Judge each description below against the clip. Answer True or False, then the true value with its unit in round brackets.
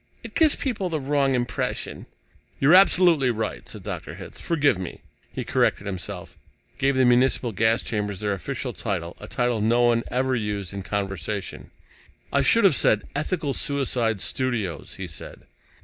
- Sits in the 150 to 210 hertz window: False (120 Hz)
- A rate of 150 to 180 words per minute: True (160 wpm)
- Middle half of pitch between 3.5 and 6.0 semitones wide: True (5.2 semitones)